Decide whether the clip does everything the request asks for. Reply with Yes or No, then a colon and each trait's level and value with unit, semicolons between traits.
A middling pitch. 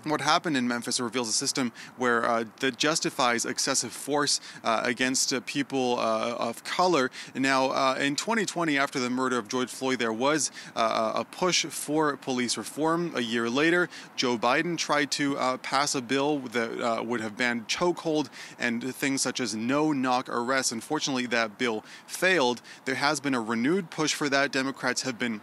No: low, 130 Hz